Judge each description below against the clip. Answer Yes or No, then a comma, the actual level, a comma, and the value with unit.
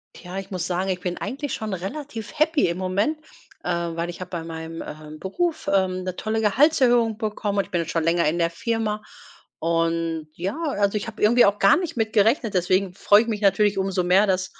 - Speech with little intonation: No, average, 4.0 semitones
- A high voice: Yes, high, 195 Hz